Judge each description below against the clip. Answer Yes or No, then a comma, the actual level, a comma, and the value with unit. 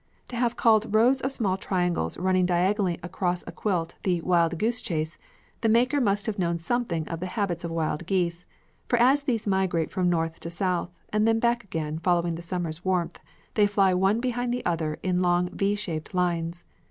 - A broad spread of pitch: No, average, 4.1 semitones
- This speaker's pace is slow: No, average, 190 wpm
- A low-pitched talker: No, medium, 185 Hz